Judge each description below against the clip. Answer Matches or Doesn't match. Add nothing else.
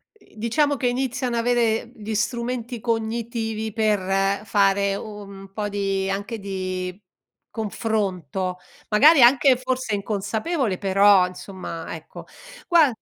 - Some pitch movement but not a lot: Matches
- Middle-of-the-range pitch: Doesn't match